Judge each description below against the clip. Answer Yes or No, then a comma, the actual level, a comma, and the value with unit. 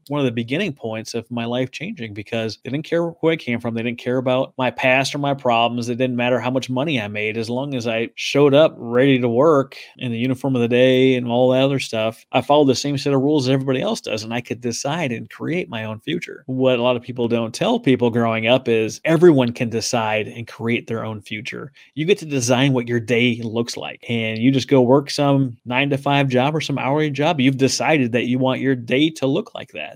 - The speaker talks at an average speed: No, fast, 255 wpm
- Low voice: Yes, low, 125 Hz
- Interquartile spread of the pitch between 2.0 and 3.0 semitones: Yes, narrow, 2.6 semitones